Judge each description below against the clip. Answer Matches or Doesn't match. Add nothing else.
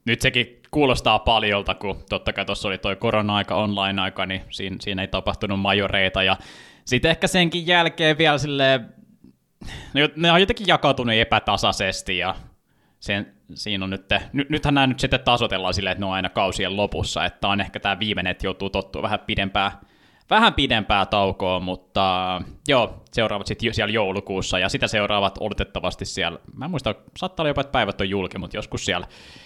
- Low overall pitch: Matches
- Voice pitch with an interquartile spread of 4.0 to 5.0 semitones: Matches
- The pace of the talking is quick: Matches